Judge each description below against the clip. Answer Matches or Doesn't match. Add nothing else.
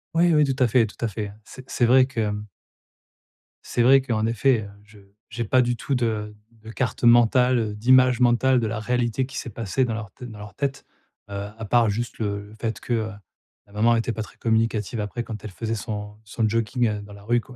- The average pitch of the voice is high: Doesn't match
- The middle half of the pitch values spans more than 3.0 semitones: Doesn't match